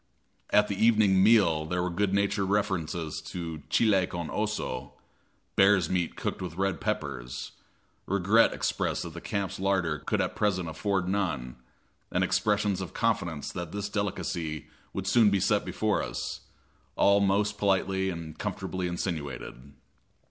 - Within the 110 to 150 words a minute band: Yes, average, 145 wpm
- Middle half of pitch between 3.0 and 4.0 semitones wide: Yes, average, 3.3 semitones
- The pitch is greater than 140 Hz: No, very low, 95 Hz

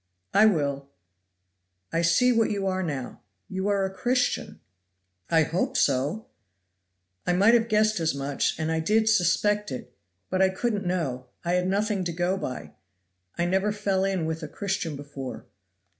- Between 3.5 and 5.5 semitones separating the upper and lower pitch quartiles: Yes, average, 4.4 semitones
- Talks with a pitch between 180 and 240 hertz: Yes, medium, 185 Hz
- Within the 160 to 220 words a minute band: Yes, average, 165 wpm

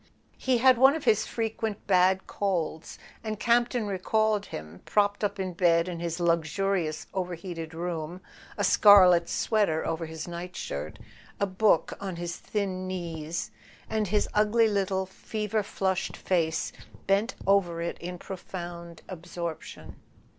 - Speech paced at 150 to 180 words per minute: No, average, 140 wpm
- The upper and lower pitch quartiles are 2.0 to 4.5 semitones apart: Yes, average, 3.5 semitones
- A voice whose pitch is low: No, medium, 185 Hz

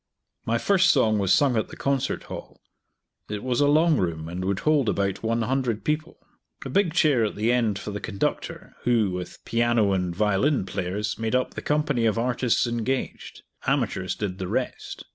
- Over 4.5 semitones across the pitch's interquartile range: Yes, average, 5.1 semitones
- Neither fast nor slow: Yes, average, 180 wpm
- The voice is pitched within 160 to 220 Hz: No, low, 115 Hz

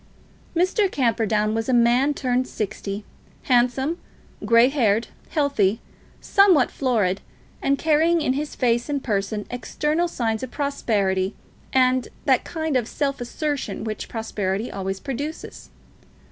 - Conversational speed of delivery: No, slow, 125 wpm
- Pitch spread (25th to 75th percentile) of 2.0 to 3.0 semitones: No, average, 4.8 semitones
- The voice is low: No, high, 245 Hz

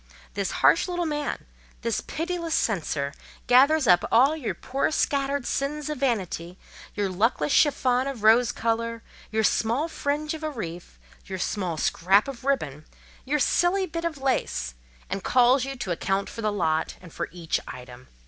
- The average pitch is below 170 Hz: No, high, 240 Hz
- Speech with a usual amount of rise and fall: No, wide, 7.1 semitones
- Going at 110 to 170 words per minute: Yes, average, 160 wpm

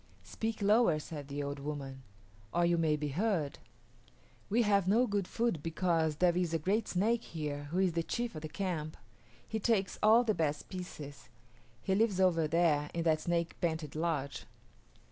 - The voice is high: No, medium, 170 Hz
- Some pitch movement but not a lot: Yes, average, 4.6 semitones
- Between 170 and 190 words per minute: Yes, average, 180 wpm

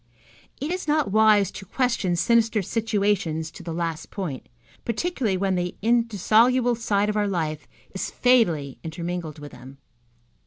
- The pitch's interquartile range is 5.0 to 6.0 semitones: Yes, wide, 5.5 semitones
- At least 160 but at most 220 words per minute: No, average, 145 wpm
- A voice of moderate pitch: No, high, 200 Hz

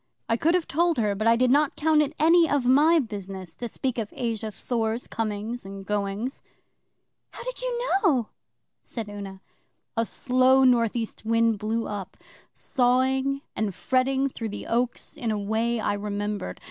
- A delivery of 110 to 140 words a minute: No, average, 170 wpm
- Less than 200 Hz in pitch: No, high, 230 Hz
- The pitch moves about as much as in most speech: Yes, average, 4.1 semitones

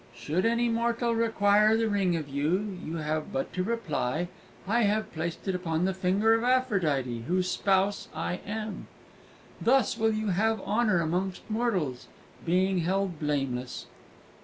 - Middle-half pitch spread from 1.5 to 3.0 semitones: No, average, 5.3 semitones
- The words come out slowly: No, average, 150 wpm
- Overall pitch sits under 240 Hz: Yes, high, 190 Hz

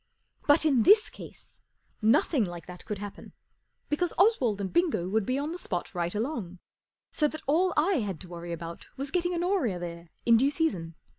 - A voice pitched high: Yes, high, 235 Hz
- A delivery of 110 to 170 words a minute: No, average, 190 wpm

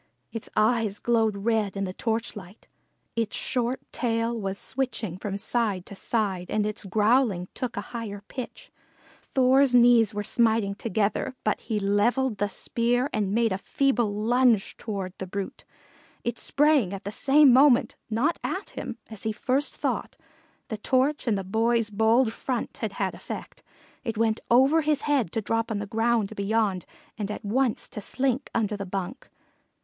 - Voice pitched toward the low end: No, high, 225 Hz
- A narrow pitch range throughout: No, average, 3.2 semitones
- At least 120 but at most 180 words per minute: Yes, average, 165 wpm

